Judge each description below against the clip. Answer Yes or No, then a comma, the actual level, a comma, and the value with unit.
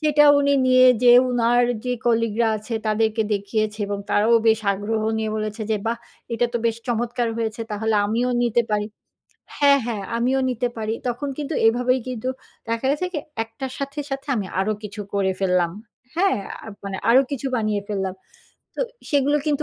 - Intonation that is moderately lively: Yes, average, 3.0 semitones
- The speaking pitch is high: Yes, high, 230 Hz